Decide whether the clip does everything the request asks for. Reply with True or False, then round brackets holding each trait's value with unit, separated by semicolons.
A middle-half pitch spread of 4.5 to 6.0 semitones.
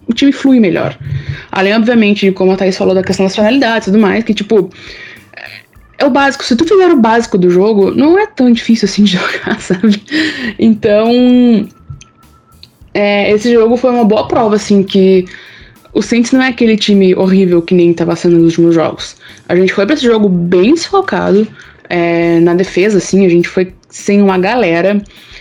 False (4.0 semitones)